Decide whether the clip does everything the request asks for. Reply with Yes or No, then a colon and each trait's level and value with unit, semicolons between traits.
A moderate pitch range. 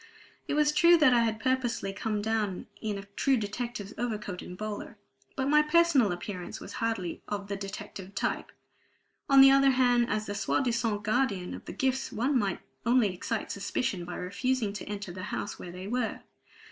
Yes: average, 4.4 semitones